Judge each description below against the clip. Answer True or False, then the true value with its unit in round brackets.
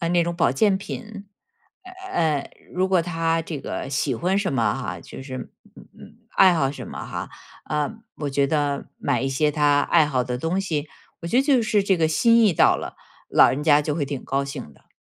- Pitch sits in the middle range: True (155 Hz)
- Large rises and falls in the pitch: False (4.7 semitones)